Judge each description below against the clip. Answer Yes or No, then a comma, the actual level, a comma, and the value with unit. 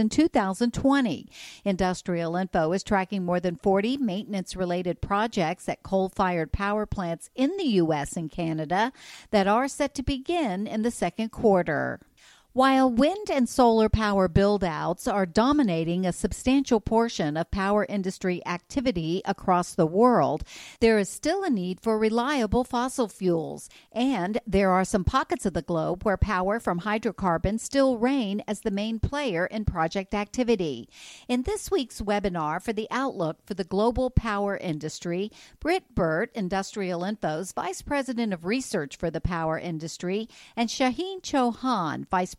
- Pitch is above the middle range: Yes, high, 205 Hz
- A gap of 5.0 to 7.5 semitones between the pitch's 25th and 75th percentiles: Yes, wide, 5.4 semitones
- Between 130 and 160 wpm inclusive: Yes, average, 150 wpm